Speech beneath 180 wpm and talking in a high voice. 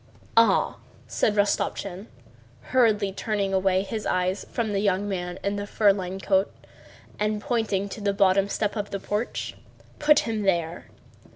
Yes: average, 155 wpm; high, 200 Hz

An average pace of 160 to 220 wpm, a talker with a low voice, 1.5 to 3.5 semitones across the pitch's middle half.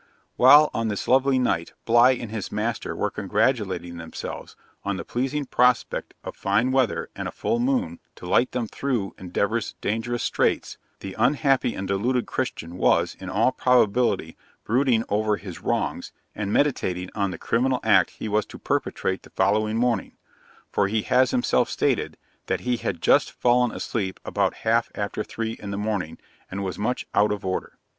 No: average, 170 wpm; low, 115 Hz; average, 4.1 semitones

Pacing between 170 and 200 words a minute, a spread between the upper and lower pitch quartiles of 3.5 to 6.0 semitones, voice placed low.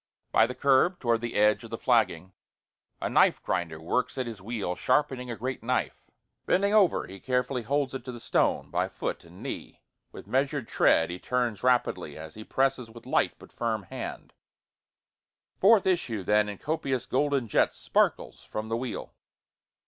Yes: average, 175 wpm; average, 3.8 semitones; low, 120 Hz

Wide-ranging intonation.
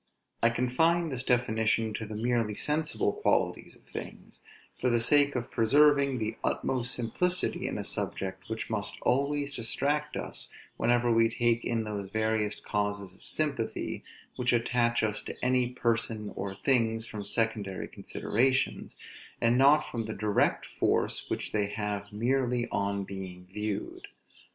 No: average, 3.2 semitones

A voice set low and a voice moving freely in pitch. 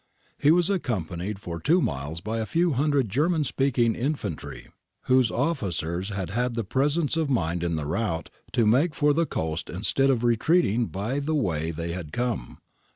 Yes: low, 120 Hz; wide, 8.5 semitones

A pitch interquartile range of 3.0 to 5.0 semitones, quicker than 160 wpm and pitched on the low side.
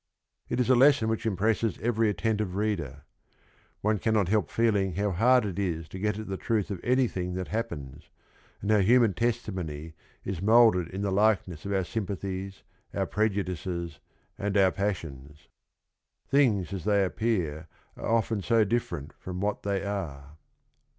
Yes: average, 3.4 semitones; average, 170 wpm; low, 100 Hz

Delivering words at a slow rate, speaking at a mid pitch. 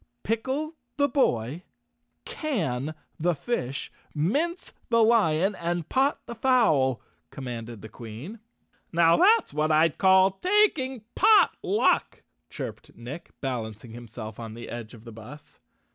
Yes: slow, 130 wpm; medium, 165 Hz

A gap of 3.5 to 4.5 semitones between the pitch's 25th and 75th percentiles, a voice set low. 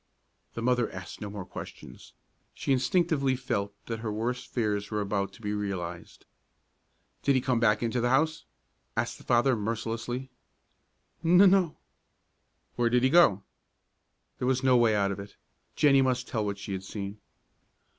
Yes: average, 4.1 semitones; low, 115 Hz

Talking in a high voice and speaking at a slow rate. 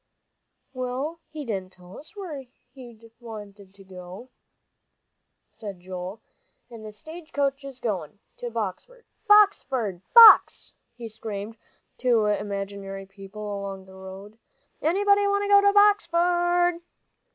Yes: high, 225 Hz; slow, 125 wpm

